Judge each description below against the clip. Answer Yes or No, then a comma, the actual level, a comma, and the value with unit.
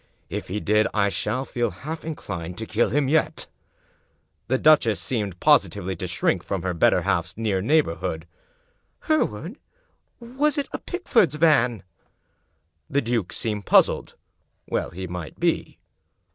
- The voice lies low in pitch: Yes, low, 115 Hz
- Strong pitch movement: Yes, wide, 8.3 semitones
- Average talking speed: Yes, average, 145 wpm